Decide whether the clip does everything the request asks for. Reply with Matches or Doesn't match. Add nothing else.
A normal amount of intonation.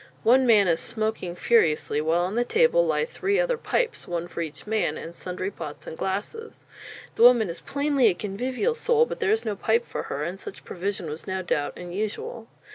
Doesn't match